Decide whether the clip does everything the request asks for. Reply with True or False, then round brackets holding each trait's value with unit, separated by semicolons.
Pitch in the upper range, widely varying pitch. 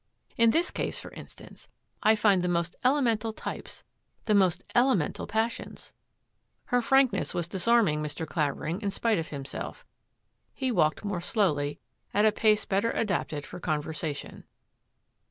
True (195 Hz; 5.9 semitones)